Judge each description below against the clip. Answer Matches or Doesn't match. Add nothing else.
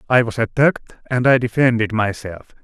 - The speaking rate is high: Doesn't match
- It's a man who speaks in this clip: Matches